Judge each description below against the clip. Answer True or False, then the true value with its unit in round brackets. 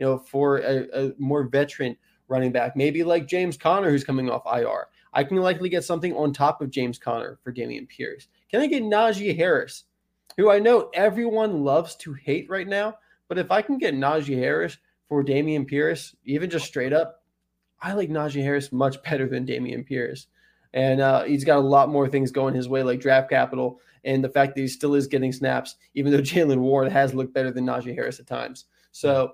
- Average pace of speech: False (210 wpm)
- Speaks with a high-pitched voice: False (140 Hz)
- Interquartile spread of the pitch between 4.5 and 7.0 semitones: False (3.9 semitones)